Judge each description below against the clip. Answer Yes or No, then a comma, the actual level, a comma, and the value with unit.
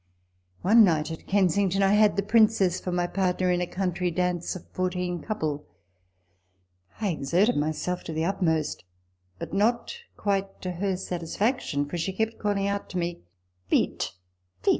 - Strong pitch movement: No, average, 2.8 semitones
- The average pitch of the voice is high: No, medium, 180 Hz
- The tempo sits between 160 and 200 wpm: Yes, average, 165 wpm